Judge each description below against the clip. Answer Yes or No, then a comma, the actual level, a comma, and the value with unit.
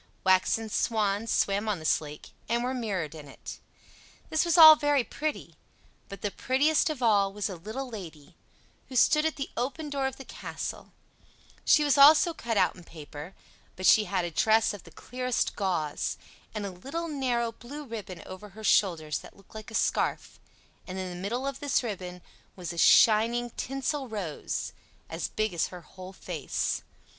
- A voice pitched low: No, high, 215 Hz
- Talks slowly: No, average, 180 wpm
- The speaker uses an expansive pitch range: Yes, wide, 6.4 semitones